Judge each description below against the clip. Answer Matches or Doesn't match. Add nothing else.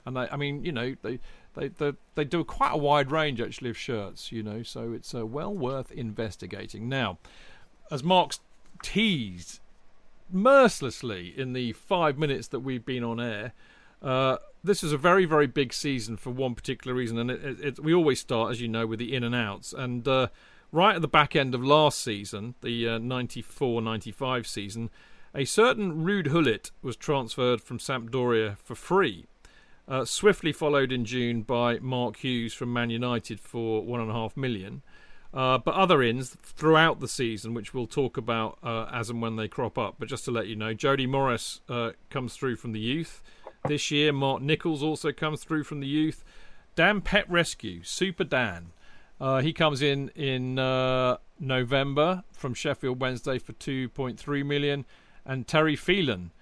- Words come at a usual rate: Matches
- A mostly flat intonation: Doesn't match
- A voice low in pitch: Matches